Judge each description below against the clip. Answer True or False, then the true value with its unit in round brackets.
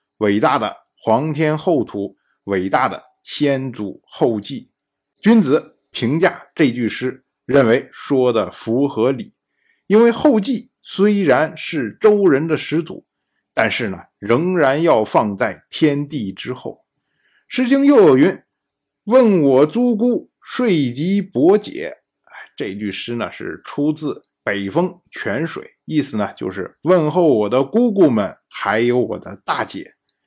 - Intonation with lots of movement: True (9.0 semitones)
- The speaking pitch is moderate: True (150 Hz)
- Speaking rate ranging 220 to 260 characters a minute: False (190 characters per minute)